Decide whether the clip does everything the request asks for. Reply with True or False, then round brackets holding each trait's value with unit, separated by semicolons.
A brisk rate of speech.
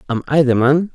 True (255 wpm)